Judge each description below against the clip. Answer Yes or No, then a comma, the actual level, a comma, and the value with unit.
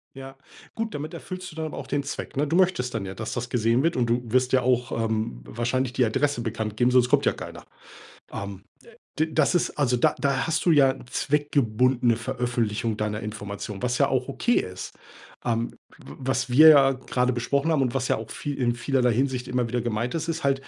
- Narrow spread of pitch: No, average, 3.3 semitones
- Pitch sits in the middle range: No, low, 125 Hz